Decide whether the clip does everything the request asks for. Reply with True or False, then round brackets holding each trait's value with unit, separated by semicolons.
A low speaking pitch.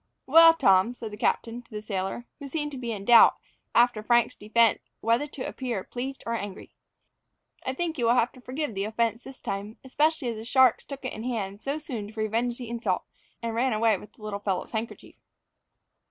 False (235 Hz)